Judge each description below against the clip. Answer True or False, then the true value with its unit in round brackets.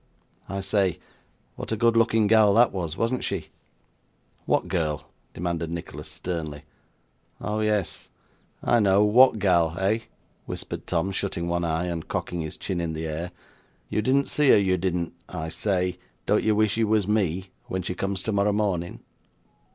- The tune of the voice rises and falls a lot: False (3.9 semitones)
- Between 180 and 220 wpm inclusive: False (165 wpm)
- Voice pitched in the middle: False (95 Hz)